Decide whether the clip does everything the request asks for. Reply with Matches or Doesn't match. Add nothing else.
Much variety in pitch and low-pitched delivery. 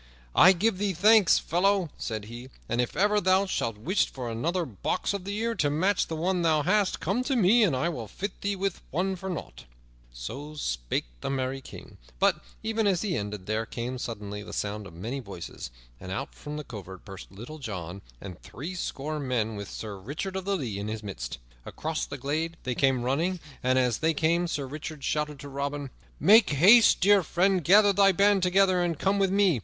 Doesn't match